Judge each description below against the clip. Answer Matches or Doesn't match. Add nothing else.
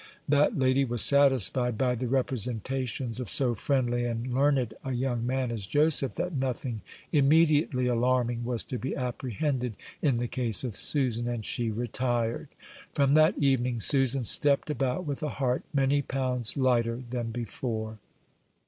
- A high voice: Doesn't match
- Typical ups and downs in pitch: Doesn't match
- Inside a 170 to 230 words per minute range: Doesn't match